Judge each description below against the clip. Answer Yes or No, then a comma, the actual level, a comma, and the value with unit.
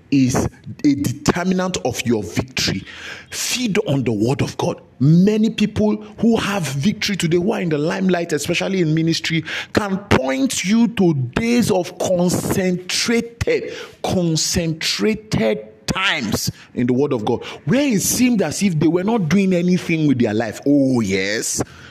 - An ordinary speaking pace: Yes, average, 150 wpm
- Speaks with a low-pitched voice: No, medium, 175 Hz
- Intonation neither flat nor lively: No, wide, 6.7 semitones